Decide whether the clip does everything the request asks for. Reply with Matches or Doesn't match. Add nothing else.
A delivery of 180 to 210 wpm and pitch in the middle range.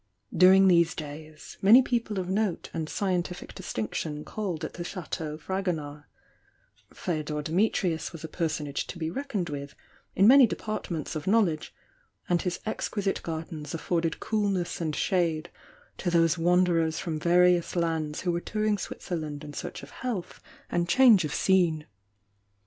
Doesn't match